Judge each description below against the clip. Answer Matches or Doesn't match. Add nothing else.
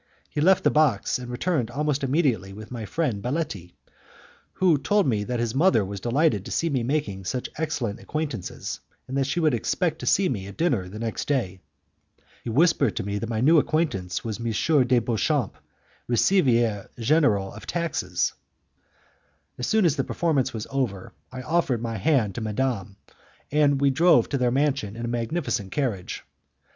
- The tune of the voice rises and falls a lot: Matches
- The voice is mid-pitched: Doesn't match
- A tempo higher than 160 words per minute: Matches